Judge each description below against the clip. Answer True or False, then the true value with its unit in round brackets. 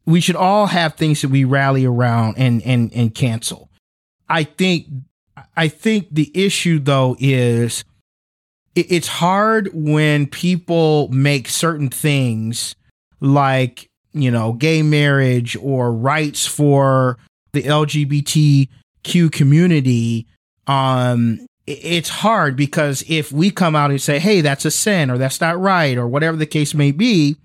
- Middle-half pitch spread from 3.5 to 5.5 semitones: True (4.1 semitones)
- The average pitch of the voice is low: False (145 Hz)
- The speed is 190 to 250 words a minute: False (140 wpm)